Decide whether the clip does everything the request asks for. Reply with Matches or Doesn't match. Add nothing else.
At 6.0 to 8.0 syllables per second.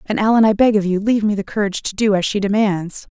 Matches